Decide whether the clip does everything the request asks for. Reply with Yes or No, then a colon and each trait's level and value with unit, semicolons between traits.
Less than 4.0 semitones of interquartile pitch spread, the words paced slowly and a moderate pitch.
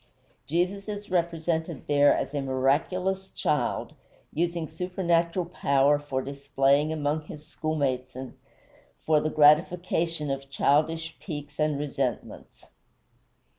Yes: average, 3.2 semitones; slow, 110 wpm; medium, 155 Hz